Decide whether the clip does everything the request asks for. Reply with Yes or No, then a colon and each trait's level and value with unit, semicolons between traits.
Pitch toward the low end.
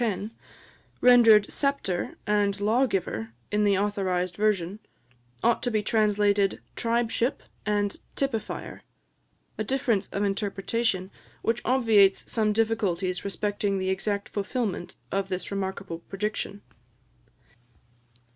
No: high, 205 Hz